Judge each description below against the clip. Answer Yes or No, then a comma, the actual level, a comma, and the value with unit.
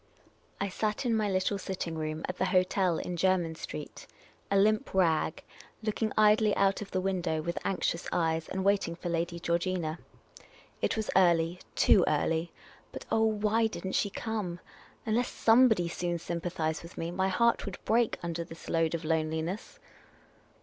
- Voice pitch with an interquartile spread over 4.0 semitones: No, average, 3.6 semitones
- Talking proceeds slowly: No, average, 170 wpm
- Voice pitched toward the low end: No, medium, 185 Hz